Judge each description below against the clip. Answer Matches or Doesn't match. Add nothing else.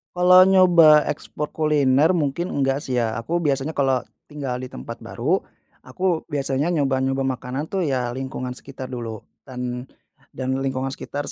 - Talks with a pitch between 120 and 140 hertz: Matches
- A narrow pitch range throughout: Doesn't match